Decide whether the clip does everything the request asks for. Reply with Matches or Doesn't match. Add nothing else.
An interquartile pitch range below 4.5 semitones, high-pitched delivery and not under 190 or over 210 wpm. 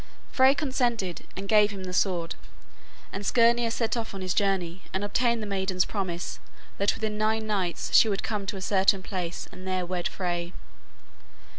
Doesn't match